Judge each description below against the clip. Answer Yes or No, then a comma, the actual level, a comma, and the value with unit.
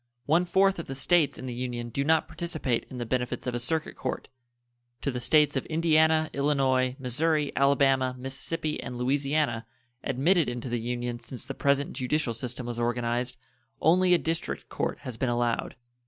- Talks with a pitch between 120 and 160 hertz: Yes, low, 135 Hz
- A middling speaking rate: Yes, average, 175 wpm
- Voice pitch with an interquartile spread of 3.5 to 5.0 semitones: Yes, average, 4.3 semitones